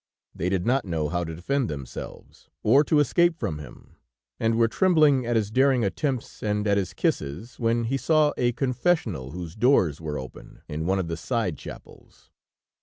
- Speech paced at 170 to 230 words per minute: Yes, average, 180 wpm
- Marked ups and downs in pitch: Yes, wide, 7.7 semitones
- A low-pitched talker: Yes, low, 110 Hz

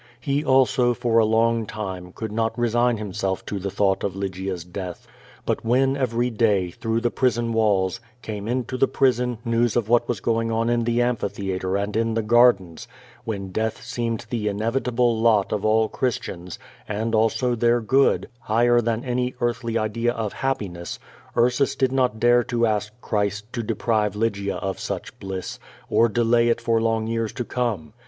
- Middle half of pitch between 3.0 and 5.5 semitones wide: No, narrow, 2.5 semitones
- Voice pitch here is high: No, low, 115 Hz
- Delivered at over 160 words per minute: Yes, average, 175 wpm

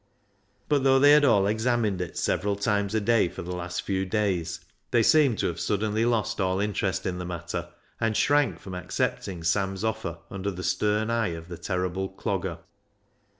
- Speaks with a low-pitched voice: Yes, low, 100 Hz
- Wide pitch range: No, average, 3.5 semitones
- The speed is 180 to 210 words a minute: Yes, average, 185 wpm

